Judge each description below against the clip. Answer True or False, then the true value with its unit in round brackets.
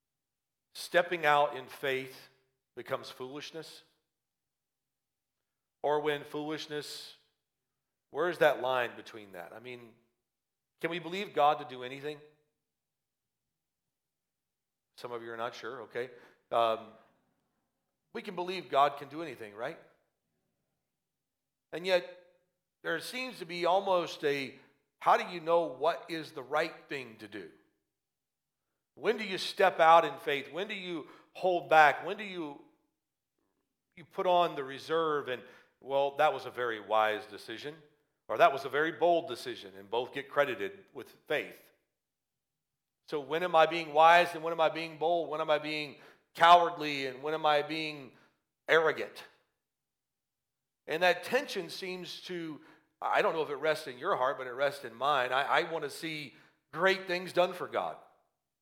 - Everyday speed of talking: True (155 wpm)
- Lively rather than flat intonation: False (4.4 semitones)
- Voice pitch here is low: False (155 Hz)